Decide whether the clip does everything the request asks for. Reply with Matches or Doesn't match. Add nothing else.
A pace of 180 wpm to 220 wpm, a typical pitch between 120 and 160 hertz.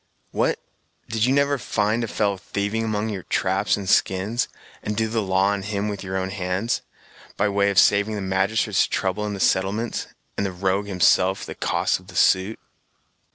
Doesn't match